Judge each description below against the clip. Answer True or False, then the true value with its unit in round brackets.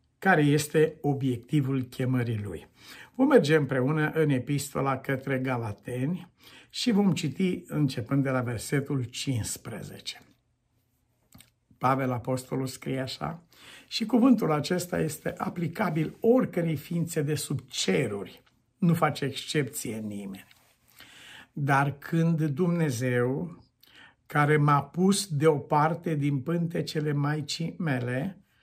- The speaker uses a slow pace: True (105 wpm)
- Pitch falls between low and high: True (145 Hz)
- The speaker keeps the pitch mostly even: False (4.3 semitones)